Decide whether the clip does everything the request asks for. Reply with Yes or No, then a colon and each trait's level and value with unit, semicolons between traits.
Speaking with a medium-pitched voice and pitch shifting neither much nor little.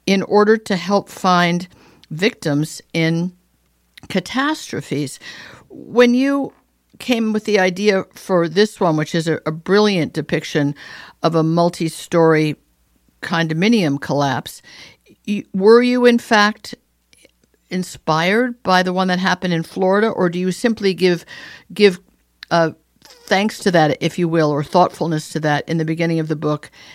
Yes: medium, 180 Hz; average, 4.6 semitones